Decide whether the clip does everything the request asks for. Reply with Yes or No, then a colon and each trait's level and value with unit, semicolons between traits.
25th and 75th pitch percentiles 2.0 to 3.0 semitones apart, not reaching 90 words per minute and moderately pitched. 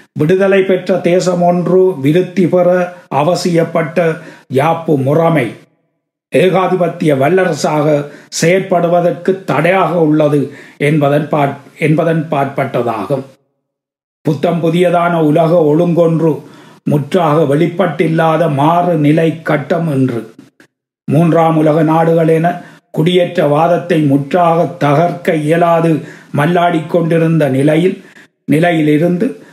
Yes: narrow, 2.6 semitones; slow, 75 wpm; medium, 165 Hz